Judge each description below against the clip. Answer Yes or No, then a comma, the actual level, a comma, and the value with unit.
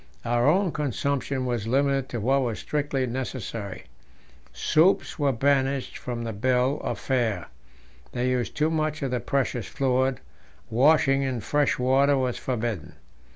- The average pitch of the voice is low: Yes, low, 130 Hz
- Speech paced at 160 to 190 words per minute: No, average, 145 wpm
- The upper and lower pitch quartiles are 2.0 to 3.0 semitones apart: Yes, narrow, 2.6 semitones